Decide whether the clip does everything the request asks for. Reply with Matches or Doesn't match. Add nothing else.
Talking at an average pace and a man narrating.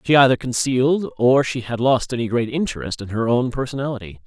Matches